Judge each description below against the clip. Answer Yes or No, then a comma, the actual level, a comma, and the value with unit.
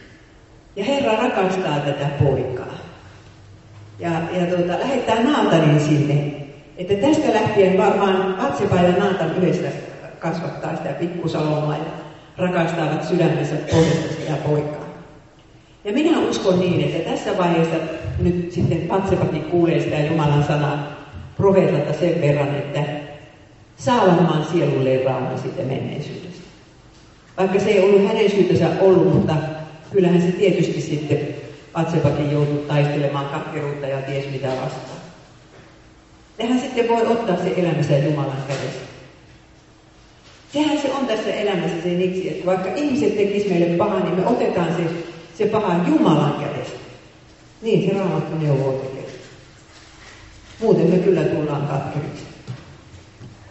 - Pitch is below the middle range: No, medium, 160 Hz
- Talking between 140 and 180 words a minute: No, average, 125 wpm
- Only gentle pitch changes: No, average, 4.2 semitones